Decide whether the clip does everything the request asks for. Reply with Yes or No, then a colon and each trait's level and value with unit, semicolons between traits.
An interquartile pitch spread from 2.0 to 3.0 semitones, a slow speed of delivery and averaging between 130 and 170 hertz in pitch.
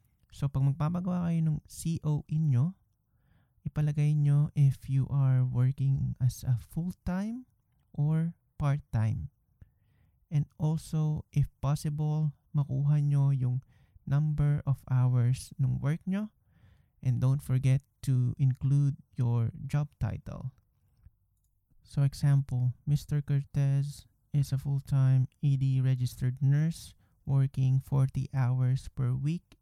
Yes: average, 2.7 semitones; slow, 110 wpm; low, 135 Hz